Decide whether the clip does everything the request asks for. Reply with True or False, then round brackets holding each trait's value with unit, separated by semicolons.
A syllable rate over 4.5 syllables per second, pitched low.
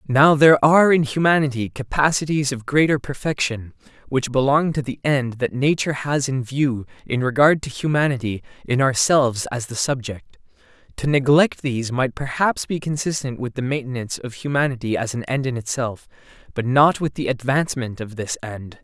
True (5.3 syllables/s; 130 Hz)